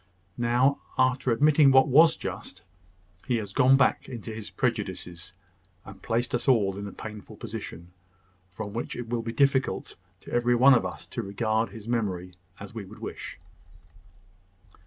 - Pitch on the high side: No, low, 115 Hz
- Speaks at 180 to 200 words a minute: No, average, 160 wpm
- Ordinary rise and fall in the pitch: Yes, average, 4.0 semitones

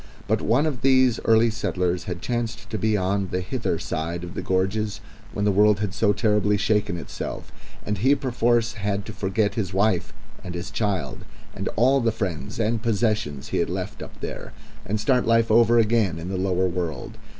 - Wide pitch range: No, average, 3.6 semitones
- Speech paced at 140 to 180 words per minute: No, average, 195 wpm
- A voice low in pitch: Yes, low, 105 Hz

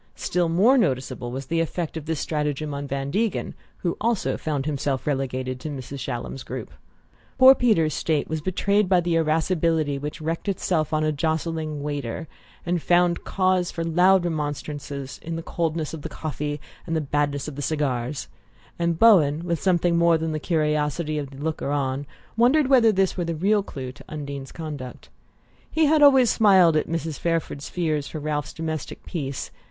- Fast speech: No, average, 180 wpm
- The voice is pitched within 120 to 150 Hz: No, medium, 160 Hz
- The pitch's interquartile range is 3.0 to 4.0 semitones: Yes, average, 3.3 semitones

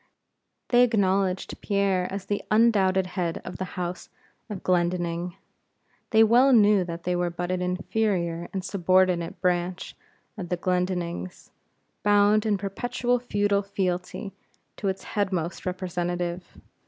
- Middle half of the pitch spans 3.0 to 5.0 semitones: No, narrow, 2.4 semitones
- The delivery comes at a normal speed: No, slow, 130 wpm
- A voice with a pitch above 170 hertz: Yes, medium, 185 Hz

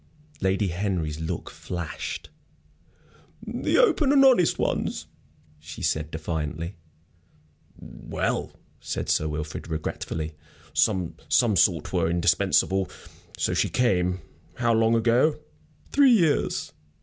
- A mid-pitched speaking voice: No, very low, 90 Hz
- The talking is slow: Yes, slow, 100 wpm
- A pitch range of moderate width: No, wide, 6.8 semitones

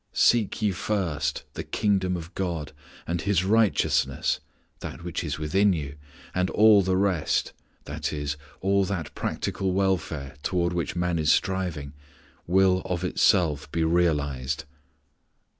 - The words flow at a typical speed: No, slow, 130 wpm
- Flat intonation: No, average, 3.7 semitones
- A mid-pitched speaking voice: No, very low, 90 Hz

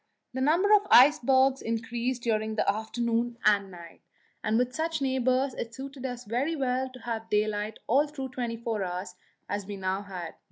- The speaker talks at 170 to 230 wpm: Yes, average, 185 wpm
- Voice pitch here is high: Yes, high, 240 Hz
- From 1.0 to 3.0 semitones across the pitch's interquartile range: No, average, 3.6 semitones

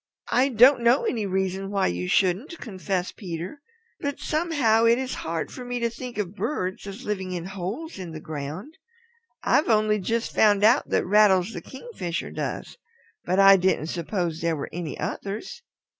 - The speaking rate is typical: Yes, average, 175 wpm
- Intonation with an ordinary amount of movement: Yes, average, 4.8 semitones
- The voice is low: No, high, 200 Hz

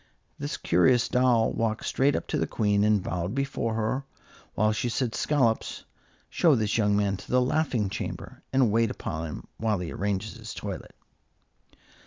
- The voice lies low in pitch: Yes, low, 110 Hz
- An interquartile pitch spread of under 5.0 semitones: Yes, average, 3.5 semitones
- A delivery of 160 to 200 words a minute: Yes, average, 170 wpm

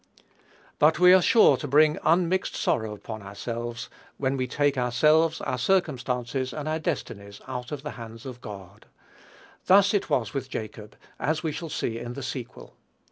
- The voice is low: Yes, low, 130 Hz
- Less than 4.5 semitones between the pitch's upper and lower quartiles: No, average, 5.0 semitones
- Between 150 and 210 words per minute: Yes, average, 170 wpm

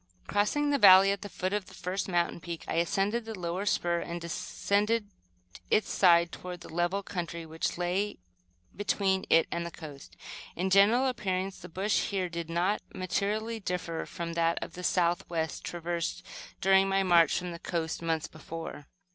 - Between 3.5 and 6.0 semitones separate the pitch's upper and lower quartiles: No, average, 2.7 semitones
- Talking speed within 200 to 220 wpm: No, average, 170 wpm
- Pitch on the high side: No, medium, 180 Hz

